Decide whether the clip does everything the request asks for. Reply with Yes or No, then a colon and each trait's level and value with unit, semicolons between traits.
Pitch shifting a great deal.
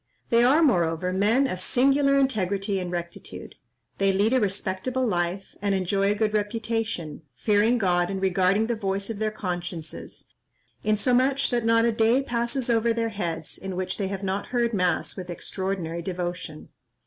No: average, 4.1 semitones